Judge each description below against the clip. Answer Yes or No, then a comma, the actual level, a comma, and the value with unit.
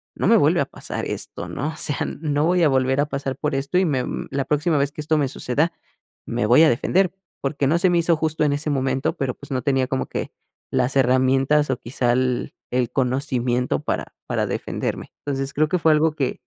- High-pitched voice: No, medium, 140 Hz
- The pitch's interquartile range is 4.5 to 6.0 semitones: No, average, 2.8 semitones